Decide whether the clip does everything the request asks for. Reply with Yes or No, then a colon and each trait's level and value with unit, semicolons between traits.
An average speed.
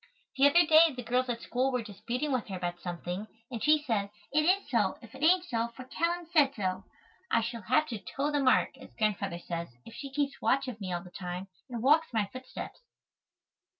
No: fast, 220 wpm